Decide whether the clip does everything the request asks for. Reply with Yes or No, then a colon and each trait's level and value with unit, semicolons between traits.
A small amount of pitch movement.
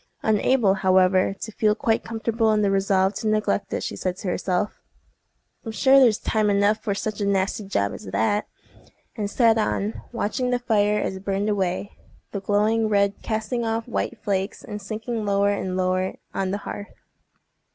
Yes: narrow, 2.2 semitones